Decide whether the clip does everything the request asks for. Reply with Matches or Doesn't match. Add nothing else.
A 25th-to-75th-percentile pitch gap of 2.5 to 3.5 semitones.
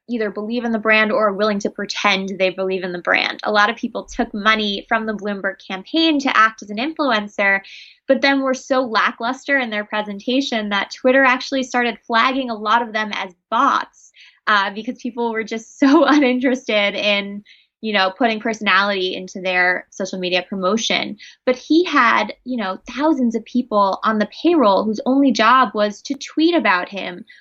Doesn't match